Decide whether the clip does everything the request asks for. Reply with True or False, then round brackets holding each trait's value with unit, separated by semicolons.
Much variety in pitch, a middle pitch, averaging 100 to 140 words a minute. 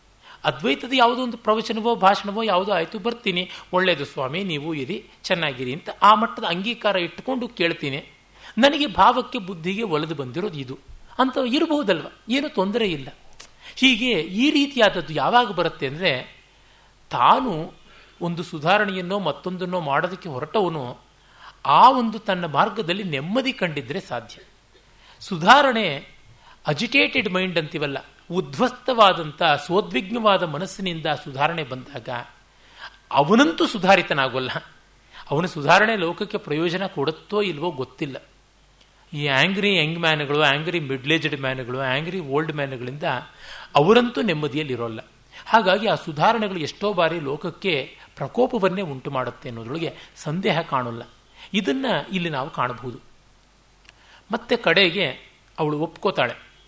True (6.5 semitones; 180 Hz; 105 wpm)